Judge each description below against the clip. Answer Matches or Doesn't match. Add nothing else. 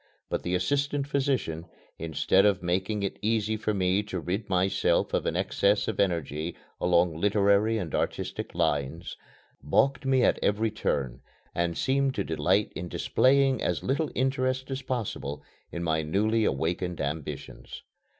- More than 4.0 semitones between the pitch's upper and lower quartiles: Matches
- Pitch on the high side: Doesn't match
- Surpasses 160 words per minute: Doesn't match